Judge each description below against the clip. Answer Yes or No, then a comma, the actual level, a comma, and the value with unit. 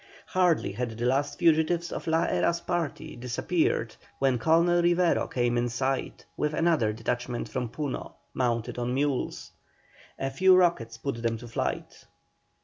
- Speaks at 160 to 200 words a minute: No, average, 145 wpm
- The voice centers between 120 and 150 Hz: Yes, low, 135 Hz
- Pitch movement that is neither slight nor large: No, wide, 5.8 semitones